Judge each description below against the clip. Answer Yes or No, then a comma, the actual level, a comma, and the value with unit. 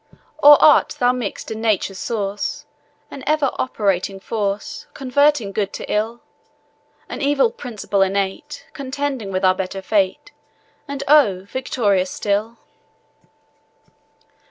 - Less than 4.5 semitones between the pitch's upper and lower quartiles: No, average, 5.3 semitones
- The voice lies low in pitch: No, high, 220 Hz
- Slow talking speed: Yes, slow, 115 wpm